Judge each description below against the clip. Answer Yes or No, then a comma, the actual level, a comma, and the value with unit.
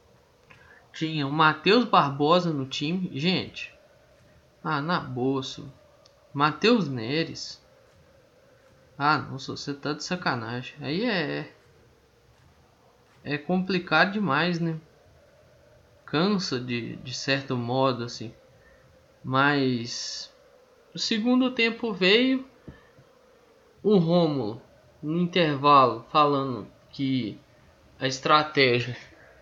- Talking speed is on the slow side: Yes, slow, 90 wpm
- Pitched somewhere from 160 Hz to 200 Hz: No, medium, 150 Hz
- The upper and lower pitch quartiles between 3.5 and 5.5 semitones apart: Yes, average, 5.2 semitones